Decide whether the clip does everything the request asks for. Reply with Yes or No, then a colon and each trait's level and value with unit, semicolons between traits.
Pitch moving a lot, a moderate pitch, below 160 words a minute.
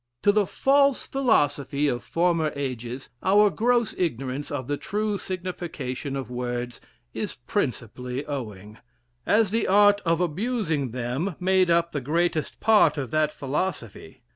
Yes: wide, 6.9 semitones; medium, 155 Hz; average, 140 wpm